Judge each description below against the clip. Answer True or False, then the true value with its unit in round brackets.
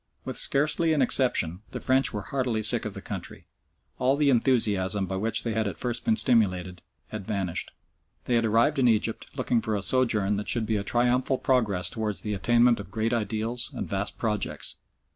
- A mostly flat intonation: False (3.4 semitones)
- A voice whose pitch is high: False (115 Hz)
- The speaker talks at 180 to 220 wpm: True (195 wpm)